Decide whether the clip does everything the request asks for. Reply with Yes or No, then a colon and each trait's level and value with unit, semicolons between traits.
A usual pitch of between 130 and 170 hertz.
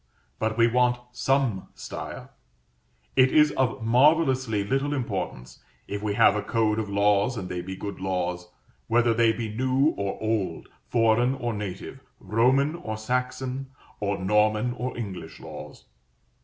No: low, 115 Hz